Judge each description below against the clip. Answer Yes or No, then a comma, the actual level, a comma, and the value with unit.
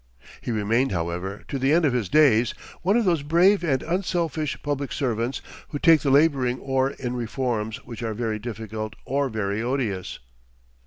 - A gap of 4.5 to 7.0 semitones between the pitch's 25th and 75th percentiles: Yes, average, 4.8 semitones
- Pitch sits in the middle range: No, low, 130 Hz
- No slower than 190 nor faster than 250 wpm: No, average, 170 wpm